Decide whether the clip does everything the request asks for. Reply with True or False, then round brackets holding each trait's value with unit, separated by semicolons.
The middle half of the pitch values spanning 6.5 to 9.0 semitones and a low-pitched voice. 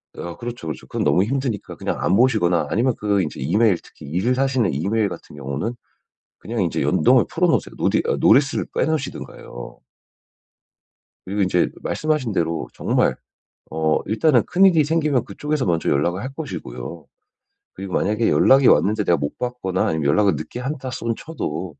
True (7.0 semitones; 105 Hz)